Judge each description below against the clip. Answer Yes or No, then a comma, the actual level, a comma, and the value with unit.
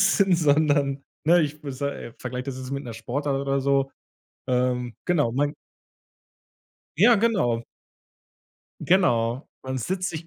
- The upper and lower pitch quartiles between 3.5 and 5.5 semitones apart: Yes, average, 4.3 semitones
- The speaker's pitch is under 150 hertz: Yes, medium, 140 Hz